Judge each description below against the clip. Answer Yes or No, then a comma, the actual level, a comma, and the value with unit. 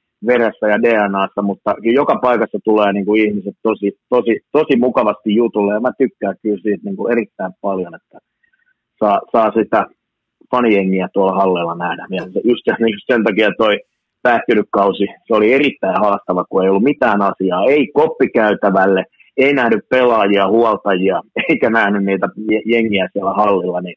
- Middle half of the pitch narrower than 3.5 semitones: Yes, average, 2.9 semitones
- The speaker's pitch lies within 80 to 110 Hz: Yes, low, 105 Hz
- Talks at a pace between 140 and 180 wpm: Yes, fast, 155 wpm